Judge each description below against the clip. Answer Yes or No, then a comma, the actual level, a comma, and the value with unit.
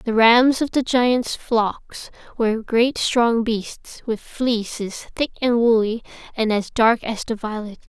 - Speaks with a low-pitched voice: No, high, 230 Hz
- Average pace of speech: Yes, average, 160 wpm